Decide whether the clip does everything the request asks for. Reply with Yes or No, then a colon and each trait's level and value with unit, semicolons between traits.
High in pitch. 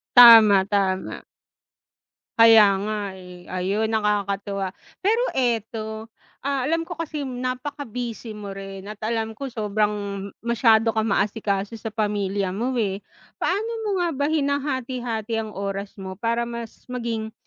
Yes: high, 220 Hz